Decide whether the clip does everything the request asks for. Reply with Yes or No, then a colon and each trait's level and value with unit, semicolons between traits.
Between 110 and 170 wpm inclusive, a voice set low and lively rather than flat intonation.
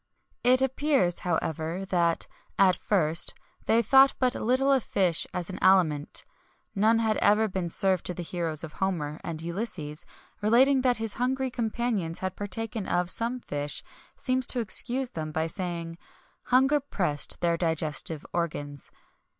No: average, 150 wpm; high, 190 Hz; wide, 6.3 semitones